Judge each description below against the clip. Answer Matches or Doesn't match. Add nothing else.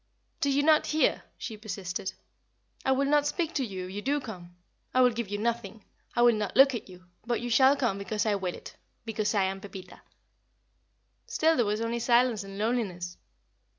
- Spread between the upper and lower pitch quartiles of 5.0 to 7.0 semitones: Doesn't match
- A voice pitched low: Doesn't match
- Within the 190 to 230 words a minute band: Matches